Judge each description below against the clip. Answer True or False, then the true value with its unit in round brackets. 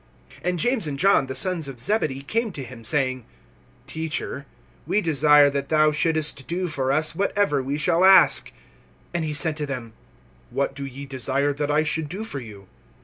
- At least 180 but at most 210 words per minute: True (185 wpm)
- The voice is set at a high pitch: False (150 Hz)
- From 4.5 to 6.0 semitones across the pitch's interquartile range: False (3.4 semitones)